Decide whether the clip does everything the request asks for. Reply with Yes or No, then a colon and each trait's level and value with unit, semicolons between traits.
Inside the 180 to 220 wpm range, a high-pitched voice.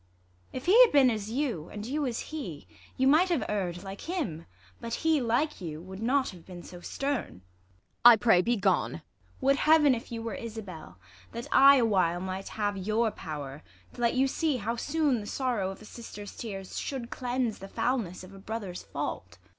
Yes: average, 200 wpm; high, 225 Hz